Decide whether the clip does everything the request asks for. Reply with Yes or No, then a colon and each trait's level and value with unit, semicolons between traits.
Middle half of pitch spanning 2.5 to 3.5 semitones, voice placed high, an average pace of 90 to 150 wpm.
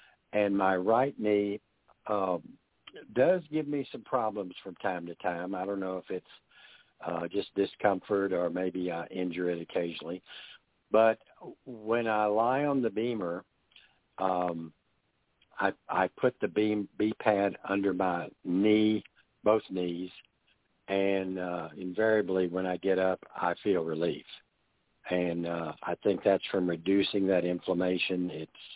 No: average, 2.9 semitones; very low, 95 Hz; average, 140 wpm